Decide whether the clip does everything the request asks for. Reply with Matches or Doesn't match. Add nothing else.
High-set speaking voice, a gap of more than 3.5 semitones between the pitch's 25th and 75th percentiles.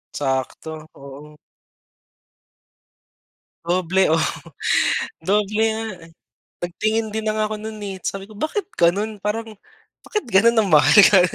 Matches